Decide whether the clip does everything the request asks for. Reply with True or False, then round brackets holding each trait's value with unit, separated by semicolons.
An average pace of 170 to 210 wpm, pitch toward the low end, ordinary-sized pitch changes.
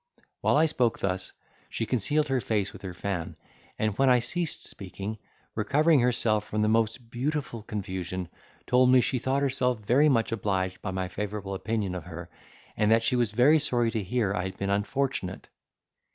True (180 wpm; 110 Hz; 4.4 semitones)